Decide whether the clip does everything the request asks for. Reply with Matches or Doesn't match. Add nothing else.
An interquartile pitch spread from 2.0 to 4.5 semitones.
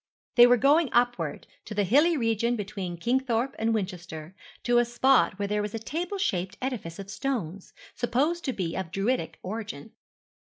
Doesn't match